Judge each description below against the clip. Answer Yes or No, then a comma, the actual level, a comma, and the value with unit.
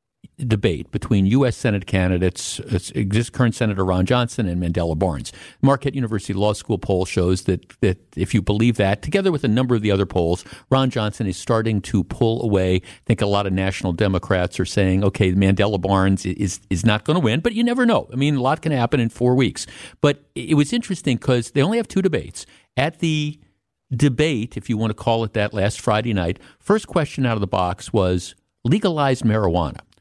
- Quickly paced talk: Yes, fast, 210 wpm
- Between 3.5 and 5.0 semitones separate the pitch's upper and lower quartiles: No, wide, 5.4 semitones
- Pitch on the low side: Yes, low, 110 Hz